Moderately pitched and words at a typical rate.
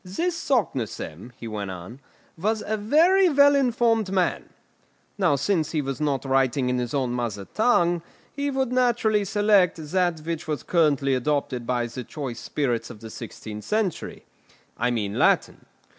Yes: medium, 155 Hz; average, 160 wpm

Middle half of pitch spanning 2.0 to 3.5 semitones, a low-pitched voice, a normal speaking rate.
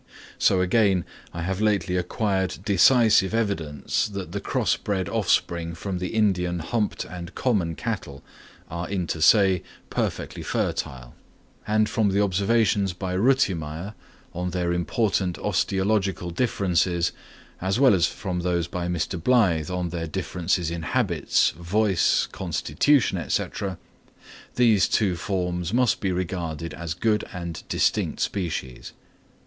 No: average, 3.2 semitones; very low, 90 Hz; slow, 125 wpm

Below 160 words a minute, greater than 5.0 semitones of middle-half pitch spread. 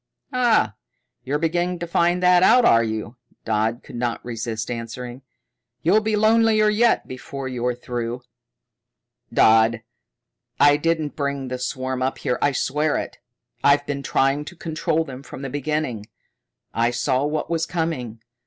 Yes: average, 150 wpm; wide, 5.4 semitones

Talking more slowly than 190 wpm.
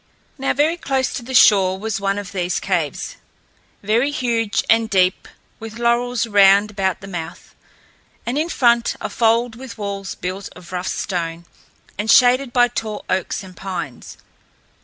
Yes: average, 160 wpm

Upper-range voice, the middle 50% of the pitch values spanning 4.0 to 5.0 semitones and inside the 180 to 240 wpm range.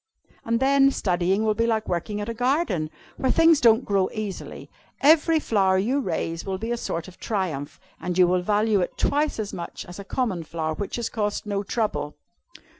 Yes: high, 210 Hz; average, 4.6 semitones; average, 195 wpm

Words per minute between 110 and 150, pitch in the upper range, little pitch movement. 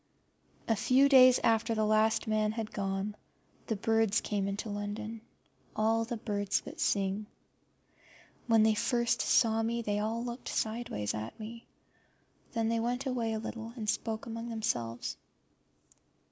Yes: average, 145 wpm; high, 220 Hz; narrow, 1.6 semitones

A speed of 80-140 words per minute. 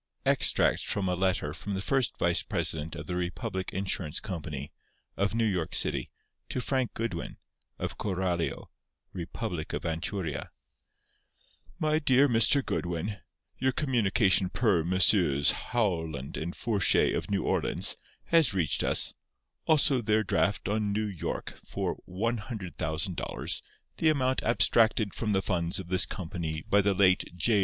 Yes: slow, 135 wpm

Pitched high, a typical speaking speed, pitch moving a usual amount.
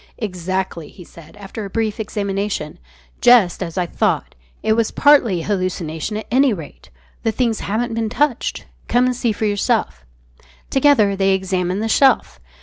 Yes: high, 205 Hz; average, 155 wpm; average, 3.7 semitones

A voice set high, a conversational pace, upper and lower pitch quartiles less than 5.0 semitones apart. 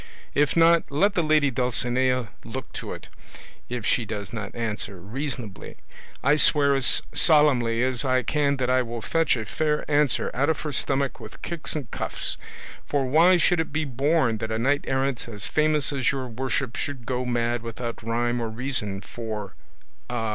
No: low, 130 Hz; average, 180 wpm; average, 3.8 semitones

